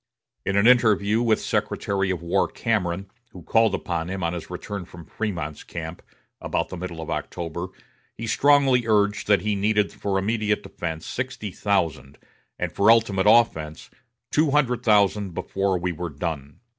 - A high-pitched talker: No, low, 100 Hz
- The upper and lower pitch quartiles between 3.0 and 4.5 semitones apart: Yes, average, 4.1 semitones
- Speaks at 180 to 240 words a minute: No, average, 160 wpm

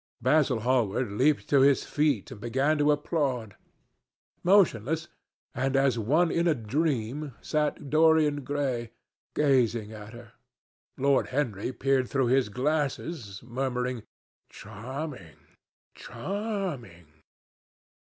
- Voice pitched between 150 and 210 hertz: No, low, 135 Hz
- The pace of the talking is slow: Yes, slow, 105 wpm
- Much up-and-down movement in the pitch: No, average, 4.2 semitones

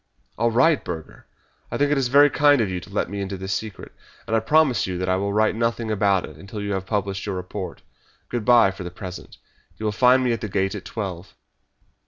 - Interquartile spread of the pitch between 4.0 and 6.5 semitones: No, average, 3.6 semitones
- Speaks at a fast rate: Yes, fast, 240 wpm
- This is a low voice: Yes, low, 105 Hz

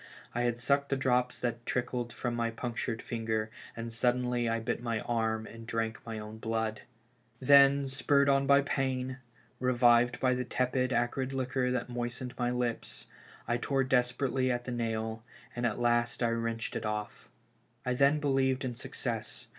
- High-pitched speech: No, low, 120 Hz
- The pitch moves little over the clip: Yes, narrow, 2.0 semitones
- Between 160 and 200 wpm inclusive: Yes, average, 170 wpm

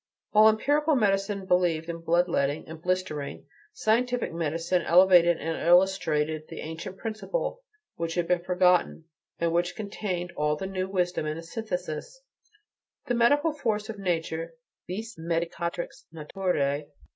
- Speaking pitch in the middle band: Yes, medium, 180 Hz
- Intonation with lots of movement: No, average, 3.7 semitones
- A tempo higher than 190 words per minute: No, slow, 135 wpm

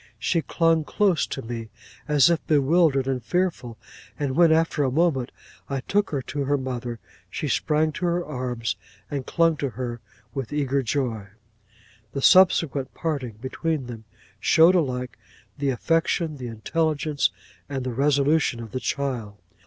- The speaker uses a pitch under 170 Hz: Yes, medium, 140 Hz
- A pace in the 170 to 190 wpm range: No, average, 155 wpm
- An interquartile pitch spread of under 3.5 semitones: No, average, 4.3 semitones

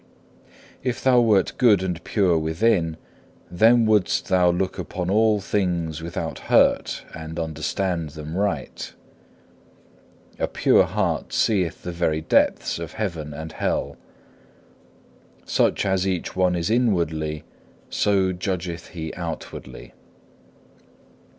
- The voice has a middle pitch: No, very low, 90 Hz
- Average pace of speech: No, slow, 120 wpm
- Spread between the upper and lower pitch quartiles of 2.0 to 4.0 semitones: Yes, average, 3.5 semitones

